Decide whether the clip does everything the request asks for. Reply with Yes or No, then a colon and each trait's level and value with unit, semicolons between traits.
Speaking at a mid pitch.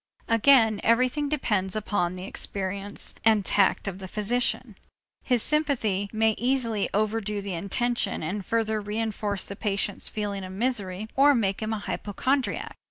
No: high, 215 Hz